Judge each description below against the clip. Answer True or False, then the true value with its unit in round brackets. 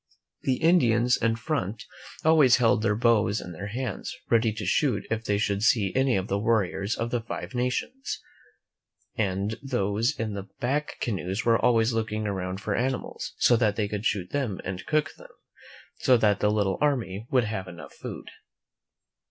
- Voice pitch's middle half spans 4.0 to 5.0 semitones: False (3.5 semitones)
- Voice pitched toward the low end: True (110 Hz)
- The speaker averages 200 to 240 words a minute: False (175 wpm)